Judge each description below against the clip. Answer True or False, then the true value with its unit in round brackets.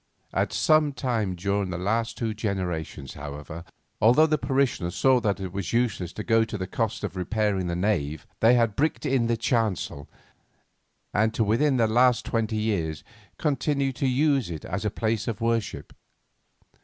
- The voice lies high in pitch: False (110 Hz)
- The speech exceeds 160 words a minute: True (170 wpm)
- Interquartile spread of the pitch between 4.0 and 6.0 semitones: True (4.6 semitones)